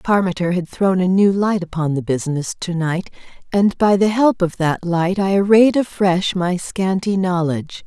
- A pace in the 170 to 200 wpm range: Yes, average, 175 wpm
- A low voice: No, medium, 185 Hz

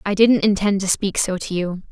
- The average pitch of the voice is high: Yes, high, 195 Hz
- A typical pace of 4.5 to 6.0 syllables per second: Yes, 5.1 syllables/s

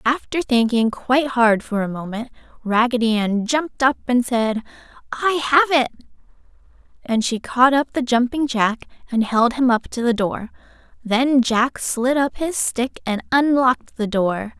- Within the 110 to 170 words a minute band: Yes, average, 165 wpm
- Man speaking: No, female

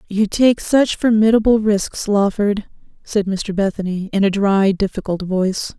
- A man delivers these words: No, female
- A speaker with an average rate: Yes, average, 145 wpm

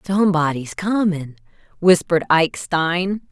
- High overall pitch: No, medium, 175 Hz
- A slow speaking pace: Yes, slow, 90 wpm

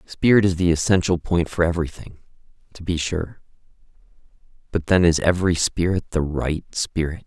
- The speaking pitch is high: No, very low, 85 Hz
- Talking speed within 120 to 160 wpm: Yes, average, 150 wpm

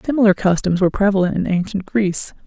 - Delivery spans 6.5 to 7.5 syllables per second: Yes, 6.7 syllables/s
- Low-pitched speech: No, high, 195 Hz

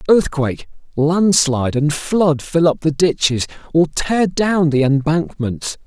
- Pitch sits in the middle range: Yes, medium, 155 Hz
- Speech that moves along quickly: No, slow, 135 wpm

